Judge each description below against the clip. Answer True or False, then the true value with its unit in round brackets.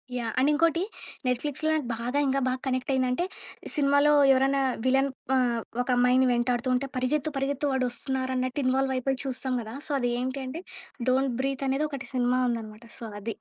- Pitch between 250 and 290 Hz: True (260 Hz)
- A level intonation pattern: True (1.7 semitones)